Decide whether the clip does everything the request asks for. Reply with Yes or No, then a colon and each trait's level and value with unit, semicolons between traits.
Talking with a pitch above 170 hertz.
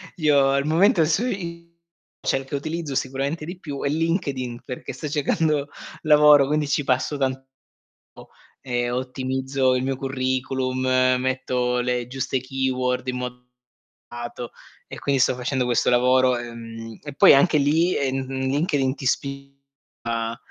No: low, 135 Hz